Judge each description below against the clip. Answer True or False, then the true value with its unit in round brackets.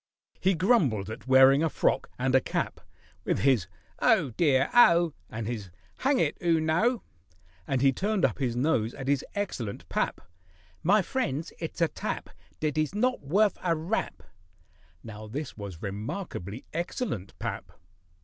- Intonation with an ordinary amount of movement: False (7.0 semitones)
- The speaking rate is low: False (155 wpm)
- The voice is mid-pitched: True (145 Hz)